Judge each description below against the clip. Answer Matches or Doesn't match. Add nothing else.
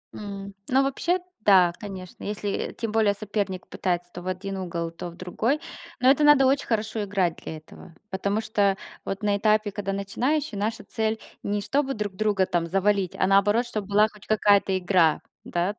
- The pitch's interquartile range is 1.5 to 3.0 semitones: Matches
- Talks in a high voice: Matches